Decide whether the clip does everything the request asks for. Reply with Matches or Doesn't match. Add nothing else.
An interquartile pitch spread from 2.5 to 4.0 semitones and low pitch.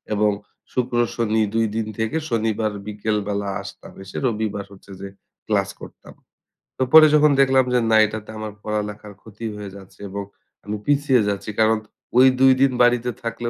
Matches